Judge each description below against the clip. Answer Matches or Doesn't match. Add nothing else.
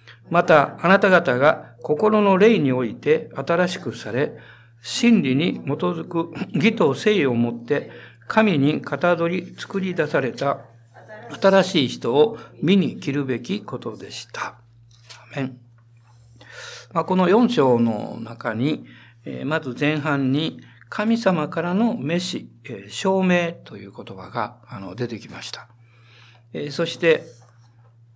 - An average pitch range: Doesn't match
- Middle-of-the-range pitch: Matches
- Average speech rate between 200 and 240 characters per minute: Matches